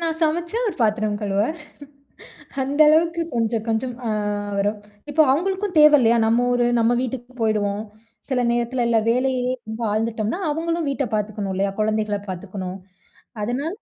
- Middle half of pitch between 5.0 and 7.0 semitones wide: Yes, wide, 5.4 semitones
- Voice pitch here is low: No, high, 240 Hz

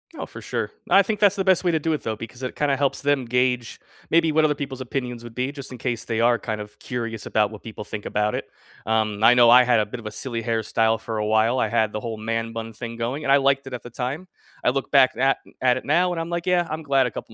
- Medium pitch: No, low, 125 Hz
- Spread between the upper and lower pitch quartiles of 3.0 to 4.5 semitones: Yes, average, 3.7 semitones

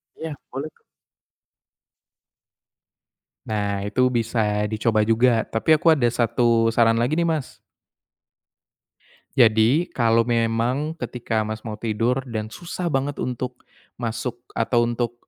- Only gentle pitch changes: Yes, narrow, 2.2 semitones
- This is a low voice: Yes, low, 120 Hz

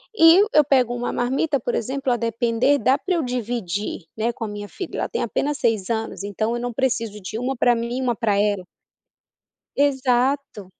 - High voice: Yes, high, 240 Hz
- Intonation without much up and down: No, average, 3.3 semitones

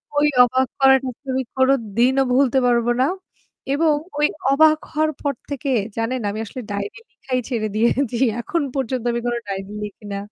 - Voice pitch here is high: Yes, very high, 255 Hz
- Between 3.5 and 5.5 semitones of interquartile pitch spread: No, average, 3.1 semitones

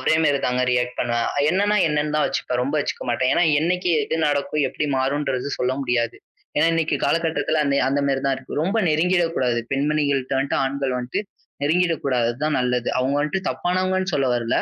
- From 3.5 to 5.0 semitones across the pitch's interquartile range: Yes, average, 3.8 semitones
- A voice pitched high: No, medium, 140 Hz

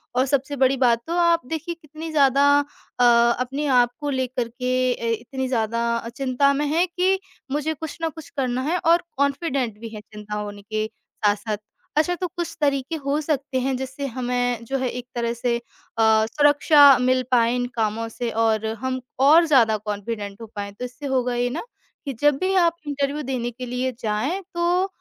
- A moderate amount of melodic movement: Yes, average, 3.9 semitones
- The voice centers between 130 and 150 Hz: No, very high, 260 Hz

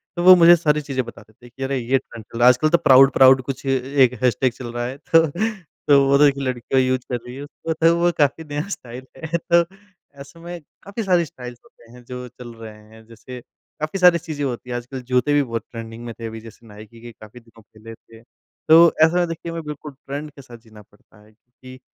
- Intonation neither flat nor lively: Yes, average, 4.5 semitones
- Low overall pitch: Yes, low, 130 Hz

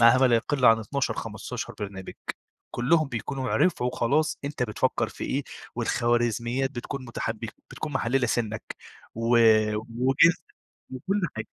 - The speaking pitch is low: Yes, low, 120 Hz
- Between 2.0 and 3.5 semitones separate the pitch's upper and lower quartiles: Yes, average, 2.7 semitones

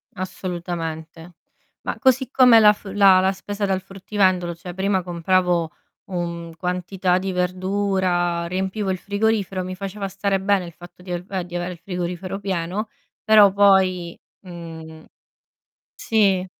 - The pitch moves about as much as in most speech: No, narrow, 2.1 semitones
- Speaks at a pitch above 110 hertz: Yes, medium, 185 Hz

